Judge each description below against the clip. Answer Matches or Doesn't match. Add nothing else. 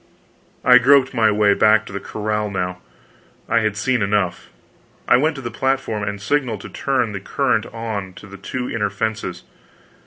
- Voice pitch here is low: Matches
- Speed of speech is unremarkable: Matches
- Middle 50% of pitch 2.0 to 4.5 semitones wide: Matches